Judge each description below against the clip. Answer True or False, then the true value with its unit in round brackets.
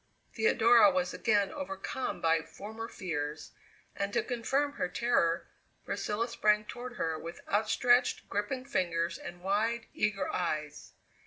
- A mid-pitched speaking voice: False (210 Hz)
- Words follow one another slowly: True (130 wpm)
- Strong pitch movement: True (5.7 semitones)